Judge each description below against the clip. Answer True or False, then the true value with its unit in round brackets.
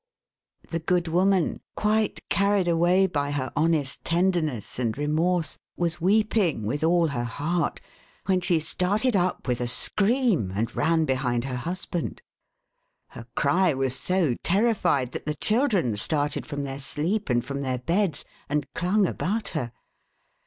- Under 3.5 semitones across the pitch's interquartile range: False (5.3 semitones)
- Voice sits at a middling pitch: True (165 Hz)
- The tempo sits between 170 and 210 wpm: False (150 wpm)